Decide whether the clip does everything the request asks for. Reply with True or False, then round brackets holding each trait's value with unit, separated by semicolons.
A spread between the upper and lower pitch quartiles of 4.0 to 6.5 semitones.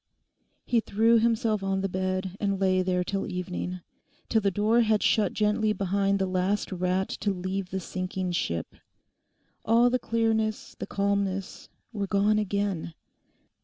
False (2.4 semitones)